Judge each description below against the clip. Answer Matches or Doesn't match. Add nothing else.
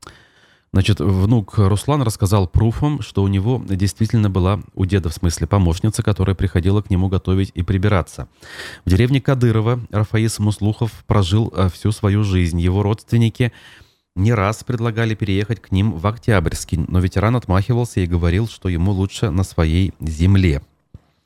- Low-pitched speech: Matches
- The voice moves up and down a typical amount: Matches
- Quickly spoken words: Doesn't match